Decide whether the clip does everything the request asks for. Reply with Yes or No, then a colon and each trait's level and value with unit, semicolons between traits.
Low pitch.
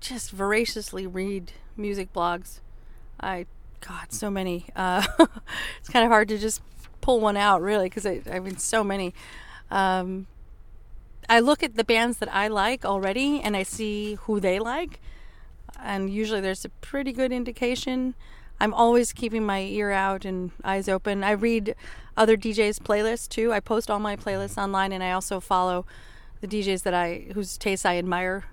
No: high, 200 Hz